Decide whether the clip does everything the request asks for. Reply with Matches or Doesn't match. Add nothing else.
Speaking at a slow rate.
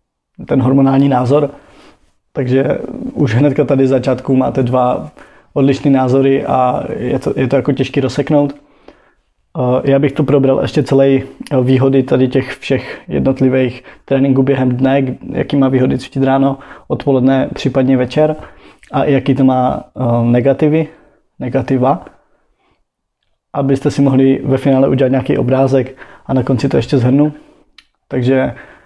Doesn't match